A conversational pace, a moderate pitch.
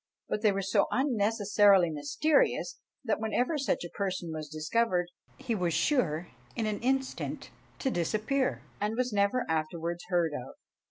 No: average, 150 wpm; high, 200 Hz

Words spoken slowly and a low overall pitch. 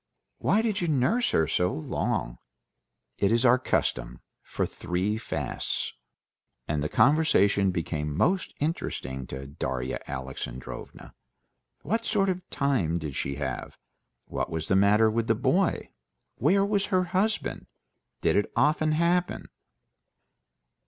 Yes: slow, 125 wpm; low, 110 Hz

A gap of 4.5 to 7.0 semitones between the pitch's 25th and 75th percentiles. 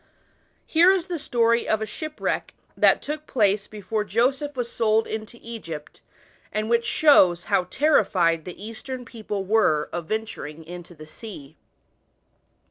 Yes: average, 5.2 semitones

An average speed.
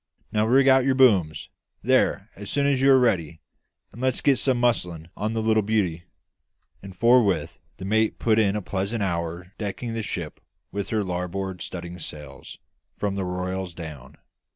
Yes: average, 175 wpm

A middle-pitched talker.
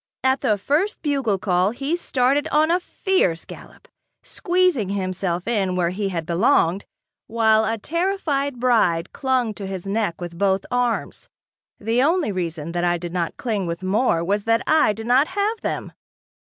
No: high, 220 Hz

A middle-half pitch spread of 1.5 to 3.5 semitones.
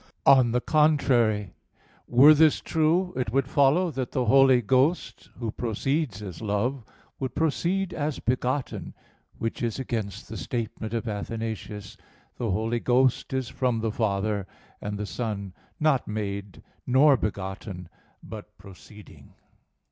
No: average, 4.3 semitones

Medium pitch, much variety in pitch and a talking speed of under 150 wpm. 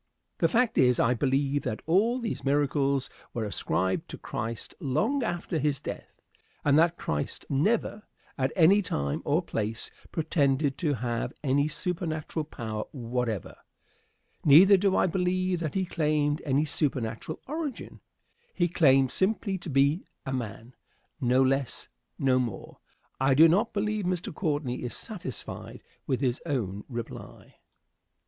Yes: medium, 145 Hz; wide, 5.8 semitones; average, 140 wpm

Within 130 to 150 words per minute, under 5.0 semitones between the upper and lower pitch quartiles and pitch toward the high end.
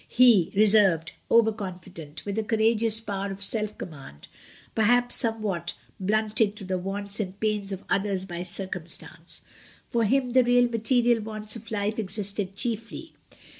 Yes: average, 145 wpm; average, 2.7 semitones; high, 210 Hz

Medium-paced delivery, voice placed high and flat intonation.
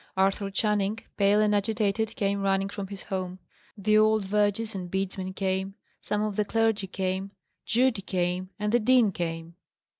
Yes: average, 160 wpm; high, 200 Hz; narrow, 1.9 semitones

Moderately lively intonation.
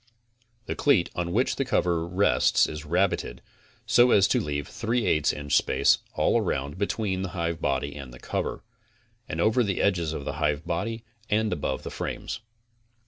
No: wide, 5.7 semitones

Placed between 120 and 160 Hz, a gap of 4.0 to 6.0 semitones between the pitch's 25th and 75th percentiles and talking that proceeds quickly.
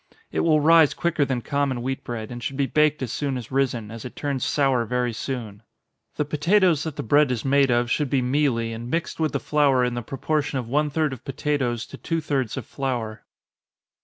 No: low, 135 Hz; average, 3.5 semitones; fast, 220 wpm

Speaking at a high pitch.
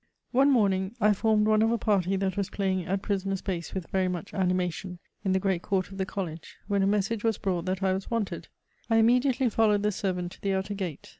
Yes: high, 195 Hz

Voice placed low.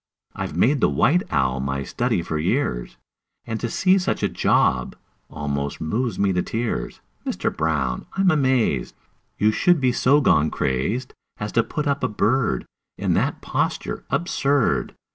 Yes: low, 110 Hz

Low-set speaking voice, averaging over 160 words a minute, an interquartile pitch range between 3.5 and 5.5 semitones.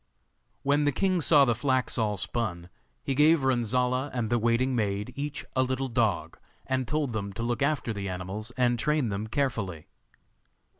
Yes: low, 120 Hz; average, 170 wpm; average, 4.0 semitones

